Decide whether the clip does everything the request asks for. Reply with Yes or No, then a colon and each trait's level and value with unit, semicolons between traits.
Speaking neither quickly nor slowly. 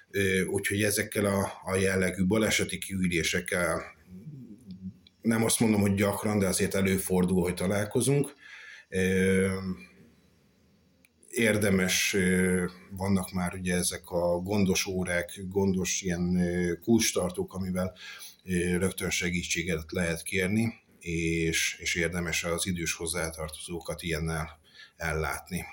No: slow, 100 wpm